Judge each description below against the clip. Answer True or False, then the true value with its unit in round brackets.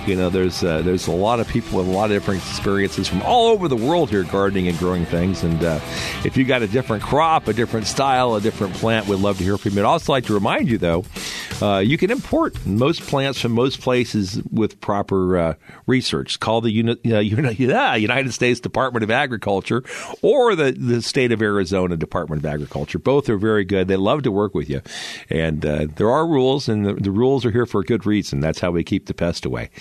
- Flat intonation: False (4.6 semitones)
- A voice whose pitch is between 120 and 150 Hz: False (105 Hz)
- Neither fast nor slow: False (235 wpm)